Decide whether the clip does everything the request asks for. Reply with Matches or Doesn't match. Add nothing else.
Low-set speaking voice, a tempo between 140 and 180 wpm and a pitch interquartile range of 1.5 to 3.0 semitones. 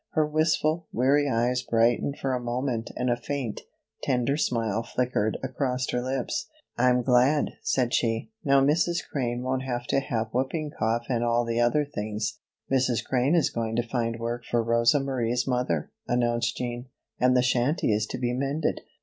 Matches